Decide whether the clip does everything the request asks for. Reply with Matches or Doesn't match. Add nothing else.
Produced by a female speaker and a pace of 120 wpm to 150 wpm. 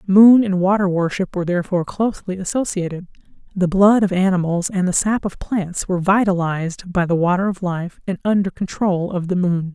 Doesn't match